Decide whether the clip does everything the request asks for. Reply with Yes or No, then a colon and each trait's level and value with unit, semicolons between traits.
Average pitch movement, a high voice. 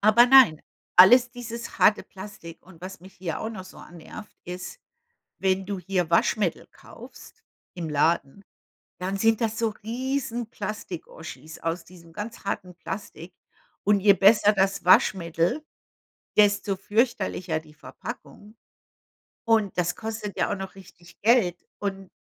Yes: average, 3.6 semitones; high, 195 Hz